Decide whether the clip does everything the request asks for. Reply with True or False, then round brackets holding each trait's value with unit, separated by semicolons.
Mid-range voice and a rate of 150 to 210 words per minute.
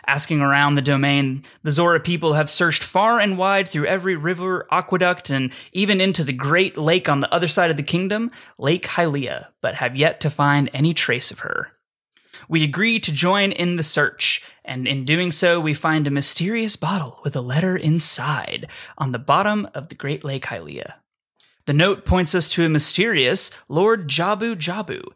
True (160 Hz; 185 wpm)